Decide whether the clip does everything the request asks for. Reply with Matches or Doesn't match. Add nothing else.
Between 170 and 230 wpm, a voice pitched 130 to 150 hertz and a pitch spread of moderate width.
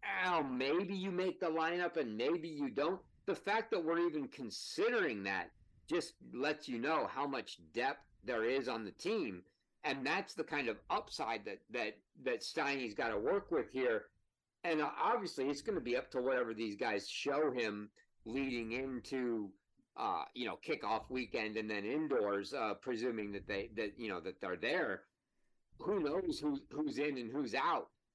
Doesn't match